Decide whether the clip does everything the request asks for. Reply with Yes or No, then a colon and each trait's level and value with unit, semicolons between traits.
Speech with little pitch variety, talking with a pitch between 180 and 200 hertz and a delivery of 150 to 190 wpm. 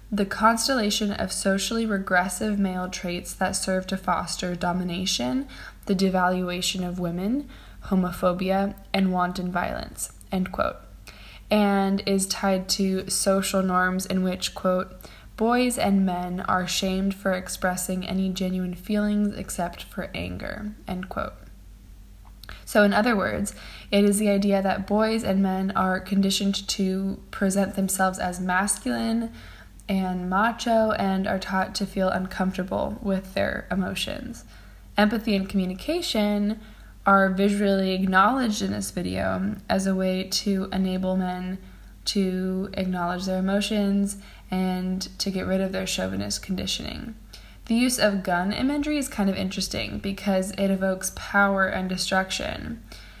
No: narrow, 1.6 semitones; high, 190 Hz; slow, 135 wpm